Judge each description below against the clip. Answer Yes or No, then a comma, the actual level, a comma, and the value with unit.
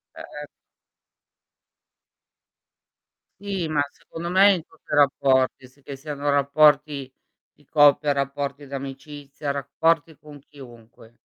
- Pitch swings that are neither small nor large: No, narrow, 1.8 semitones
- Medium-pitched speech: Yes, medium, 145 Hz